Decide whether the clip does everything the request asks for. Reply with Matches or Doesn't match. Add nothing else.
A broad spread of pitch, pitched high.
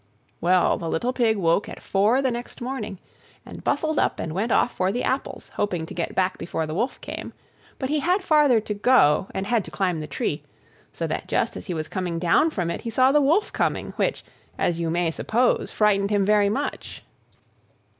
Matches